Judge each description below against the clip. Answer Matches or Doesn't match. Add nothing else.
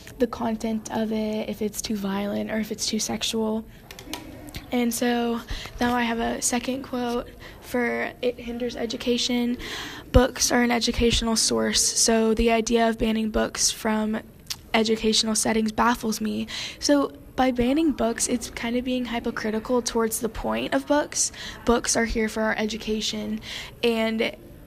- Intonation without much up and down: Matches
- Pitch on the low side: Doesn't match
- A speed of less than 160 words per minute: Matches